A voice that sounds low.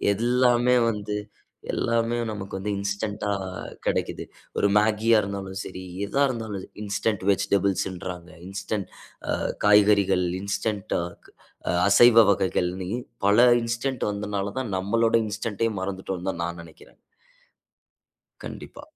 Yes: low, 100 Hz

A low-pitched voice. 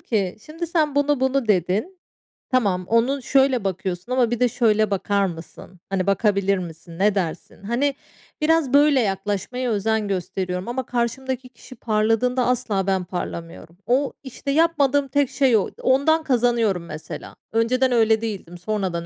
No: high, 225 Hz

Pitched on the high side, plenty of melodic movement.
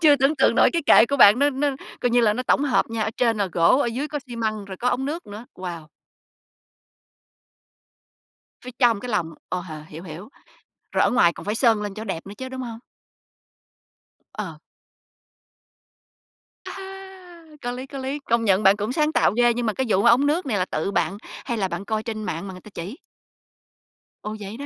No: high, 230 Hz; average, 4.8 semitones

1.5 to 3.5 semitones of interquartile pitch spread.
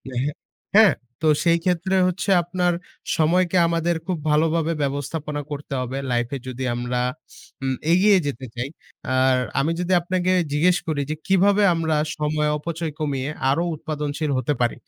No: average, 3.9 semitones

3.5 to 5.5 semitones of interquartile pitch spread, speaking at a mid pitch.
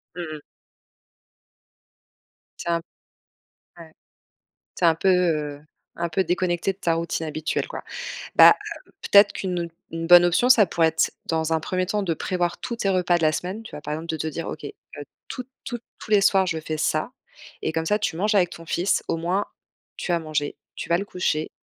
No: average, 2.8 semitones; medium, 170 Hz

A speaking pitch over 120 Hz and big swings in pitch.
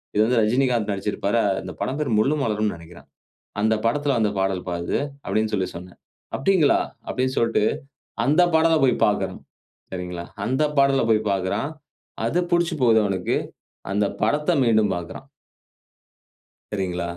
No: low, 110 Hz; wide, 5.9 semitones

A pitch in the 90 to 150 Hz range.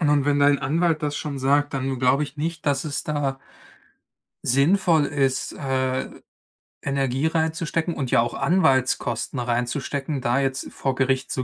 Yes: medium, 140 Hz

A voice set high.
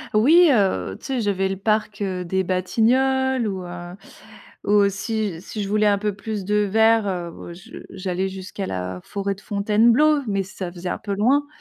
Yes: high, 200 Hz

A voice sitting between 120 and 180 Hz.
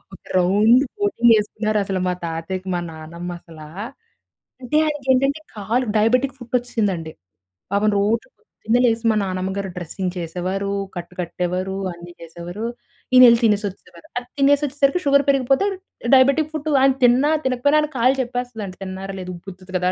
No: high, 215 Hz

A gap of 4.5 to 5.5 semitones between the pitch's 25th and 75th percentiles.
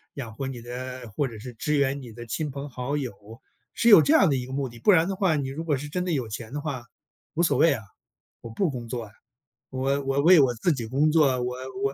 No: average, 3.5 semitones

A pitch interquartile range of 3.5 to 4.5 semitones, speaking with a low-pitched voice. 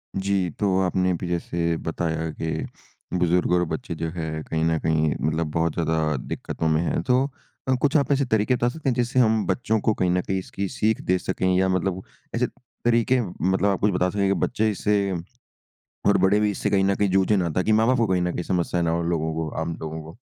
Yes: average, 4.2 semitones; very low, 90 Hz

